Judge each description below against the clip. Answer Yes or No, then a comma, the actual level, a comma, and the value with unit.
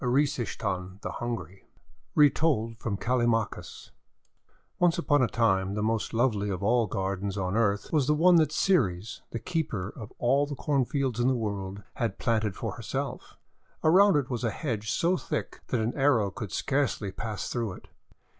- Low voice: Yes, low, 115 Hz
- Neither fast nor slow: Yes, average, 170 wpm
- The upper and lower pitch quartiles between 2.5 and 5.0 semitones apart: No, wide, 5.6 semitones